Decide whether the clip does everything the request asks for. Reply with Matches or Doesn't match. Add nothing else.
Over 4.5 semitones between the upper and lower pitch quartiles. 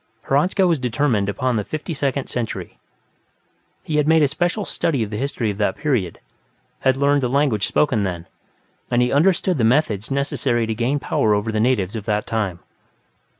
Matches